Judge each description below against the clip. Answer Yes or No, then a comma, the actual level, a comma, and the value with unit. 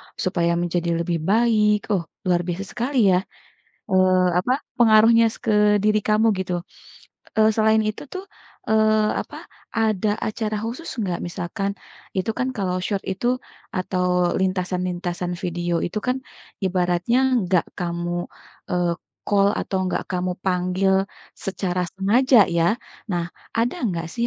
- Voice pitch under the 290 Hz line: Yes, high, 190 Hz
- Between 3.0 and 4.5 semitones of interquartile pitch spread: Yes, average, 3.4 semitones